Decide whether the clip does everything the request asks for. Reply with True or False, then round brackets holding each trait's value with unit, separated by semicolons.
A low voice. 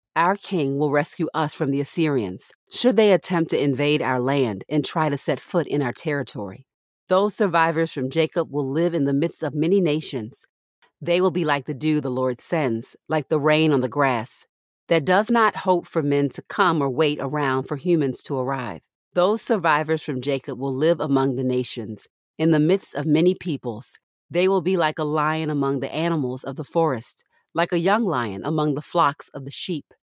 False (150 Hz)